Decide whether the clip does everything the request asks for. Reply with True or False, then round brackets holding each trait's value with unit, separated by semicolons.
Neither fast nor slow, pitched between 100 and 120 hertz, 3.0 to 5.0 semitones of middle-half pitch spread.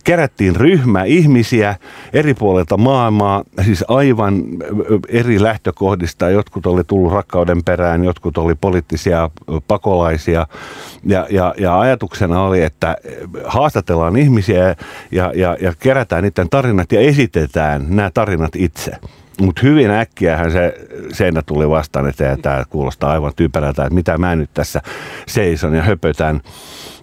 False (130 wpm; 90 Hz; 4.2 semitones)